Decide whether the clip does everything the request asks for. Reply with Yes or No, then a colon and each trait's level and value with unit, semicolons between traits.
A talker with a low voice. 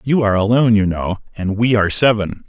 Yes: low, 105 Hz